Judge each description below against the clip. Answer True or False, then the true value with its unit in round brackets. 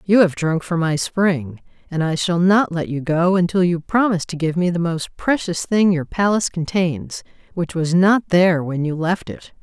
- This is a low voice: False (175 Hz)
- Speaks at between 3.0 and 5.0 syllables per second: True (4.7 syllables/s)